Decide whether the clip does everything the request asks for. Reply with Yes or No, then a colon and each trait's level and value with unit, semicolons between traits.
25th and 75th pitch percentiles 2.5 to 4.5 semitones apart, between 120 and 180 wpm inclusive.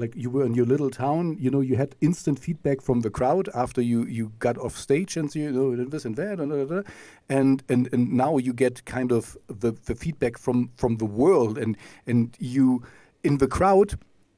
No: average, 2.9 semitones; fast, 205 wpm